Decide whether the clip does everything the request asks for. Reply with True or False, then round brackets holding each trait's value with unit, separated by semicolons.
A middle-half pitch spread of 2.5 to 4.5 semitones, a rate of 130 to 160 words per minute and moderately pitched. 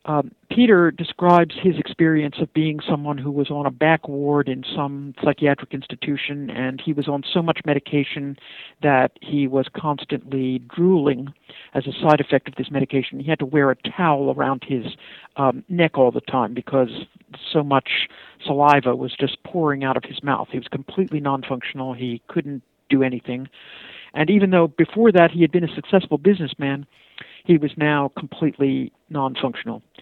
False (2.8 semitones; 170 wpm; 145 Hz)